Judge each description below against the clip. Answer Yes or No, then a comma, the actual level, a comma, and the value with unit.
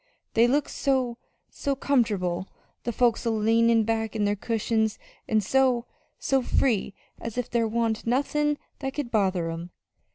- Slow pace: No, average, 155 wpm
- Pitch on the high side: Yes, high, 230 Hz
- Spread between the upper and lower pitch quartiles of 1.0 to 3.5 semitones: Yes, average, 2.9 semitones